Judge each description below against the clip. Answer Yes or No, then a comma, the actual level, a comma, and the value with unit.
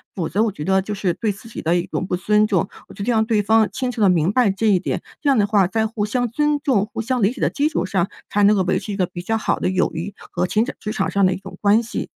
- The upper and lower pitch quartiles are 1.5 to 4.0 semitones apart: Yes, average, 3.1 semitones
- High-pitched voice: Yes, high, 205 Hz